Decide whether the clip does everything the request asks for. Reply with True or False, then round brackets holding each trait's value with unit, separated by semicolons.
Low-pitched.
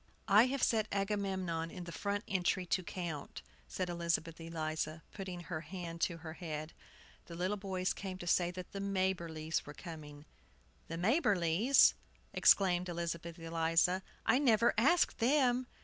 False (180 Hz)